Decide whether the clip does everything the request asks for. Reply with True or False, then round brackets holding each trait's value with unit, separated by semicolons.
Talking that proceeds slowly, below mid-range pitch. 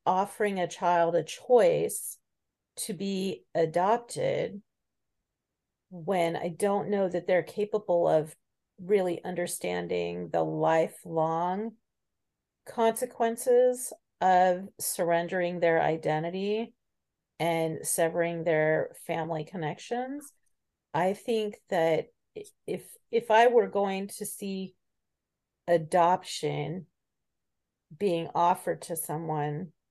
False (90 wpm; 180 Hz)